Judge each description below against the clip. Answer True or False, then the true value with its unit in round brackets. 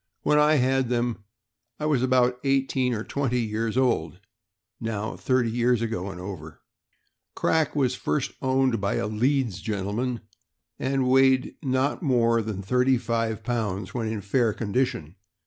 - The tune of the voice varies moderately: True (3.3 semitones)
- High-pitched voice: False (120 Hz)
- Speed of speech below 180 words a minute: True (150 wpm)